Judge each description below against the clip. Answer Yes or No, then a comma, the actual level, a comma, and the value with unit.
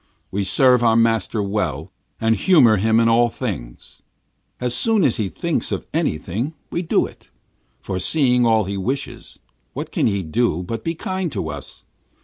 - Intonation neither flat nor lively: Yes, average, 4.5 semitones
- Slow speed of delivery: No, average, 165 wpm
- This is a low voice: Yes, low, 115 Hz